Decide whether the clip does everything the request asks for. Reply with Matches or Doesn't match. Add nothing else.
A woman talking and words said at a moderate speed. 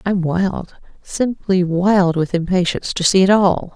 Matches